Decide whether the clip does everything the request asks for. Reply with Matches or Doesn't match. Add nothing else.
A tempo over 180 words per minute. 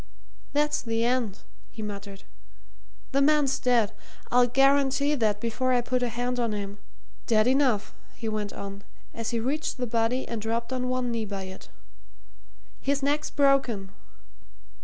Doesn't match